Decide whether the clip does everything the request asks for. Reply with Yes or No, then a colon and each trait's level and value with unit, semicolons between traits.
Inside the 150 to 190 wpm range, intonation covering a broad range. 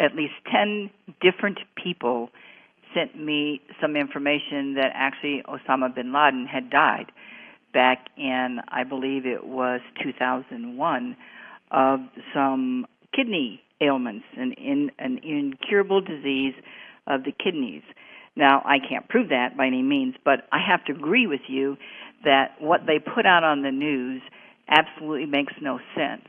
No: average, 140 wpm; wide, 6.9 semitones